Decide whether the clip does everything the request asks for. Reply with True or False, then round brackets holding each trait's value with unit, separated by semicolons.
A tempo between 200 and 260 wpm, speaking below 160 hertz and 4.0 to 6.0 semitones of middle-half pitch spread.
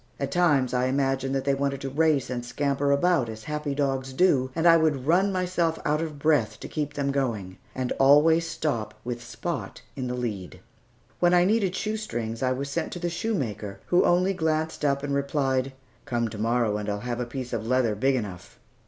True (205 wpm; 135 Hz; 4.6 semitones)